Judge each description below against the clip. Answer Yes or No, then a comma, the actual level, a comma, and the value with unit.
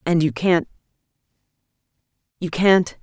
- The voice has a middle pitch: Yes, medium, 165 Hz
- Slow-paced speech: Yes, slow, 80 wpm